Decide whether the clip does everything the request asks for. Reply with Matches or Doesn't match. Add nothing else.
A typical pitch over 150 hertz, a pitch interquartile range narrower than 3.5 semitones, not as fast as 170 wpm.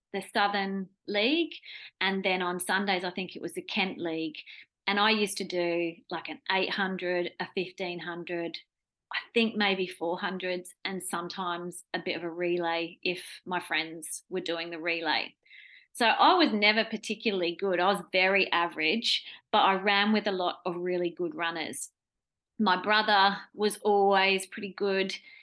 Matches